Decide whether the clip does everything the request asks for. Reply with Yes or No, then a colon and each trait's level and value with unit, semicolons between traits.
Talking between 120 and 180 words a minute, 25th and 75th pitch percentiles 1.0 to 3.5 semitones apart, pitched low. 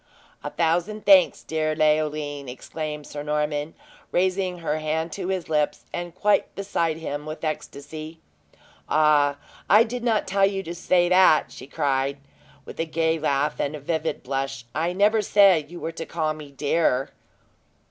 No: average, 155 wpm; average, 3.1 semitones; medium, 160 Hz